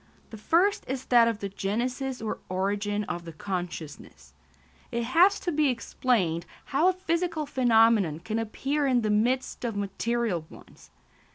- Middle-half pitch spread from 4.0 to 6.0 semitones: Yes, average, 4.8 semitones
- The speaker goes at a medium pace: Yes, average, 155 wpm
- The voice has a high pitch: Yes, high, 230 Hz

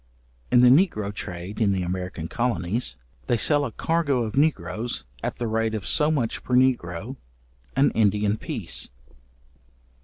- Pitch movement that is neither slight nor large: Yes, average, 4.6 semitones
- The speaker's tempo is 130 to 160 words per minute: Yes, average, 150 wpm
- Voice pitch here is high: No, low, 115 Hz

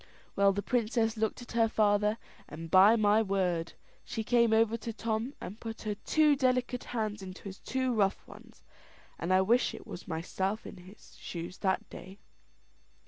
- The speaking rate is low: No, average, 180 wpm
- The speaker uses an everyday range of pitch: Yes, average, 3.3 semitones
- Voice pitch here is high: Yes, high, 215 Hz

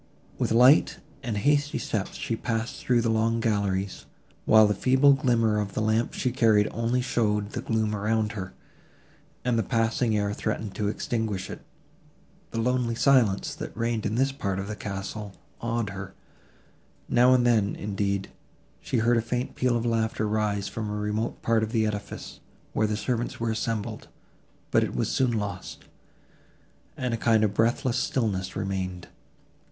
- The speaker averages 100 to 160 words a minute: No, average, 170 wpm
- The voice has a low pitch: Yes, low, 110 Hz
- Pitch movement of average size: No, narrow, 2.3 semitones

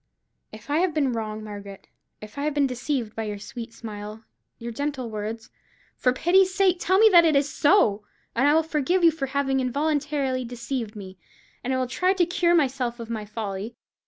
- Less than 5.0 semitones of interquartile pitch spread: No, wide, 5.4 semitones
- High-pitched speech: Yes, very high, 260 Hz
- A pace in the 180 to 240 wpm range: Yes, average, 195 wpm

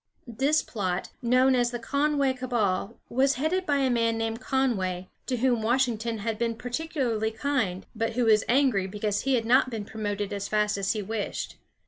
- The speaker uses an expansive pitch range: No, average, 3.6 semitones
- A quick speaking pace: No, average, 180 wpm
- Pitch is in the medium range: No, high, 230 Hz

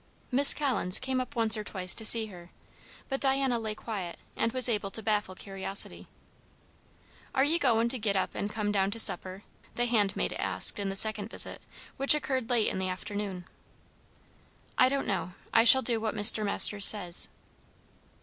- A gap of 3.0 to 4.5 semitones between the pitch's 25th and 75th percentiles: Yes, average, 3.7 semitones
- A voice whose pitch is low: No, high, 215 Hz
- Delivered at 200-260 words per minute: No, average, 180 wpm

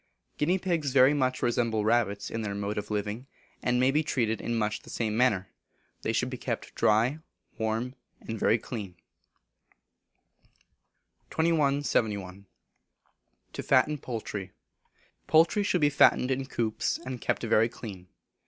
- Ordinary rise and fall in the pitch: Yes, average, 4.5 semitones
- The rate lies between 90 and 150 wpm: Yes, average, 140 wpm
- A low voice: Yes, low, 120 Hz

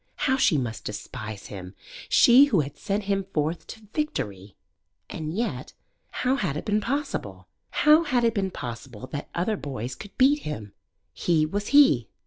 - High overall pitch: No, medium, 175 Hz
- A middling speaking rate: Yes, average, 165 wpm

